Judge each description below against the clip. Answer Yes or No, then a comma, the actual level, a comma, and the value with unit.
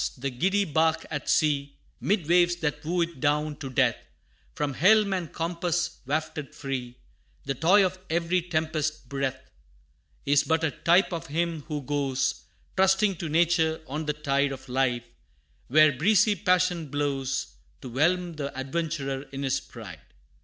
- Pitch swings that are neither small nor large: Yes, average, 3.8 semitones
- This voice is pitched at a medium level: Yes, medium, 155 Hz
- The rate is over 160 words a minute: No, average, 155 wpm